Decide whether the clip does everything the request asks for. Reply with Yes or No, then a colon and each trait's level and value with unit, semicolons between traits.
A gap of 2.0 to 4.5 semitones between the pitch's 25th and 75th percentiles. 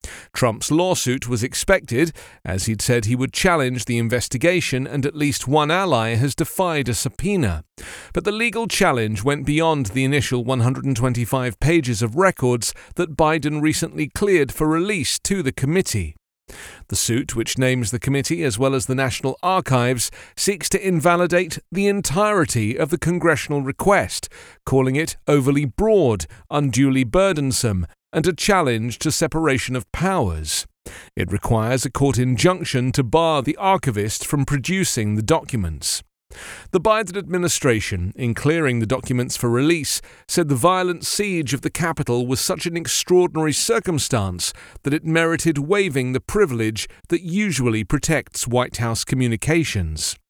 No: wide, 5.4 semitones